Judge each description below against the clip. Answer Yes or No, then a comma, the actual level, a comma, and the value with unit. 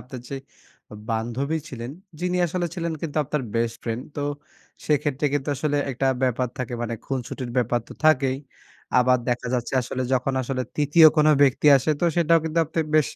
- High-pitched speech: No, low, 135 Hz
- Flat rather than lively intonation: No, average, 3.5 semitones